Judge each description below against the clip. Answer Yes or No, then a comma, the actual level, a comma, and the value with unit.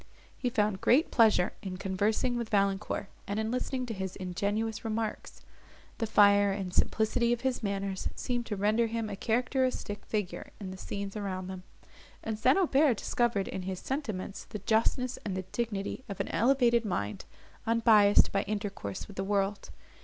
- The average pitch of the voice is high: Yes, high, 210 Hz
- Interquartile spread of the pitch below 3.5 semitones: Yes, average, 3.1 semitones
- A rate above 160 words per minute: Yes, average, 170 wpm